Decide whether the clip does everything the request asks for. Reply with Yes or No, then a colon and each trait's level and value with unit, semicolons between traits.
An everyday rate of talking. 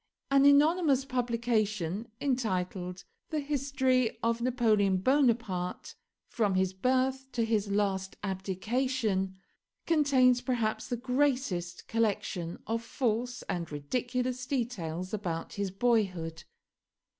No: slow, 100 wpm